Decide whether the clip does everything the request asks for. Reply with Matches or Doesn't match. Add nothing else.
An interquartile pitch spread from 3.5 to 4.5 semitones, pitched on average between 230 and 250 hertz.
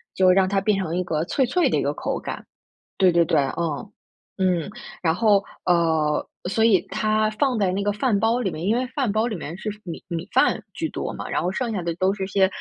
Doesn't match